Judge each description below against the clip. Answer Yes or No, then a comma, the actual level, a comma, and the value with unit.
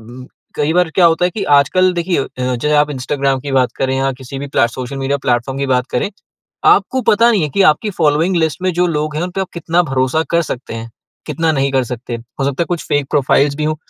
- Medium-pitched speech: Yes, medium, 145 Hz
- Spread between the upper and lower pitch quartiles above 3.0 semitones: Yes, average, 4.3 semitones